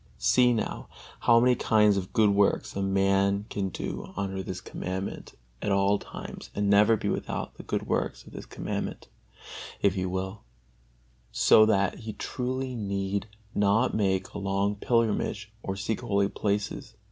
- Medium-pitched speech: No, low, 100 Hz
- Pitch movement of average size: No, narrow, 1.9 semitones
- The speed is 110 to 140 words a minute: No, average, 160 wpm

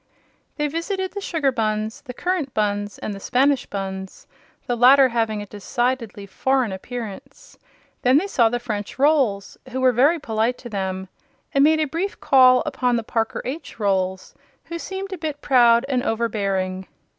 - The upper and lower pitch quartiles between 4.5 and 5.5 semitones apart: Yes, average, 5.2 semitones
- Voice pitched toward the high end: Yes, high, 245 Hz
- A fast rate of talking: No, average, 170 wpm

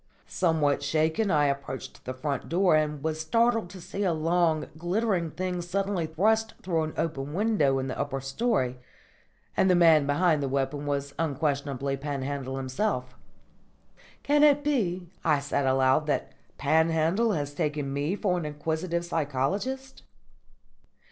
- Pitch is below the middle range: No, medium, 155 Hz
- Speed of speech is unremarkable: Yes, average, 150 wpm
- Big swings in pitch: No, average, 4.5 semitones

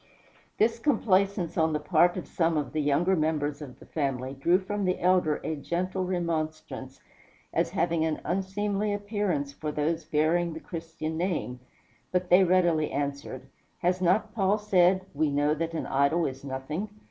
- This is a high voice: No, medium, 165 Hz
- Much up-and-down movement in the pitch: No, average, 3.8 semitones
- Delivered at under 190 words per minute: Yes, average, 165 wpm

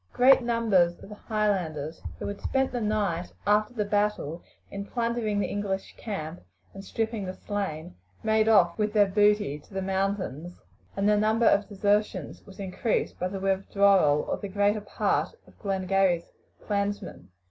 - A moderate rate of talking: Yes, average, 160 wpm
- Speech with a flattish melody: Yes, narrow, 2.0 semitones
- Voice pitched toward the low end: No, high, 200 Hz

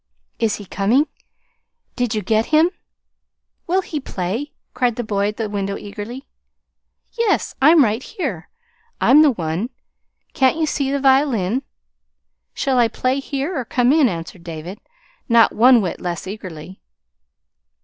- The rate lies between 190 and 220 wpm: No, average, 145 wpm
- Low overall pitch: No, high, 235 Hz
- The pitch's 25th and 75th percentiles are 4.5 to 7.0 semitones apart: Yes, wide, 5.5 semitones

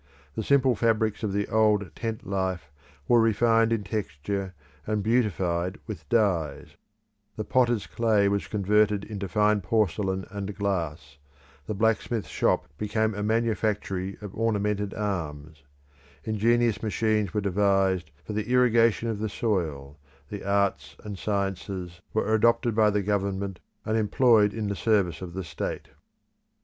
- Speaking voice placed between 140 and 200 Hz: No, low, 105 Hz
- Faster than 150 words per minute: No, average, 140 wpm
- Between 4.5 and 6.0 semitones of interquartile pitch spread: No, narrow, 2.5 semitones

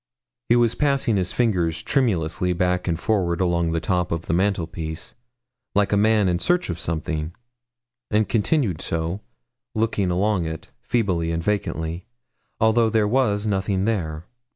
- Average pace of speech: Yes, average, 150 wpm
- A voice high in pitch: No, very low, 95 Hz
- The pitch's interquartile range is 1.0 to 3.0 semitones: No, average, 4.6 semitones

